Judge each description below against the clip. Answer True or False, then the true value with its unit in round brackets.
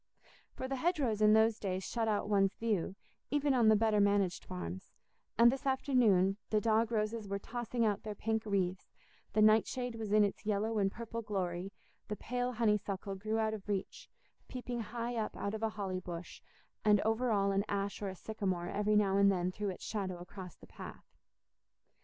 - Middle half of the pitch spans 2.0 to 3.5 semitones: True (2.4 semitones)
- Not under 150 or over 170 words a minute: False (190 wpm)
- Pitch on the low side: False (210 Hz)